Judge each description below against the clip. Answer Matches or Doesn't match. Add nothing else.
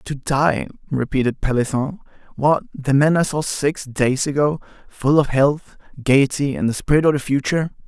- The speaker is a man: Matches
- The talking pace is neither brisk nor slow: Matches